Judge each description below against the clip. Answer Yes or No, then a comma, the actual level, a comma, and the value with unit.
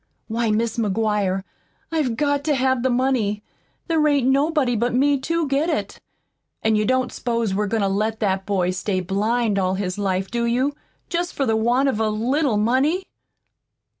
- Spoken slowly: No, average, 180 wpm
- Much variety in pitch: No, average, 4.6 semitones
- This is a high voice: Yes, high, 235 Hz